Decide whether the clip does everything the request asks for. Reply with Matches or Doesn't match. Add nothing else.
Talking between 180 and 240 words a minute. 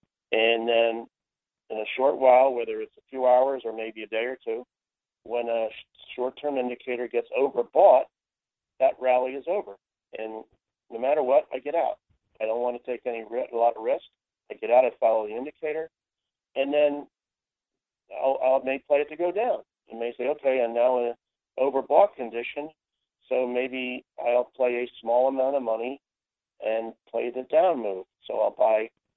Matches